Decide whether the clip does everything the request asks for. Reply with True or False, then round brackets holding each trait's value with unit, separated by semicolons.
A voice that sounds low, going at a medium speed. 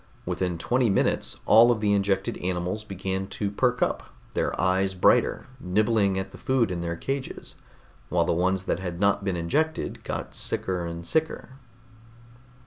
True (95 Hz; 160 wpm)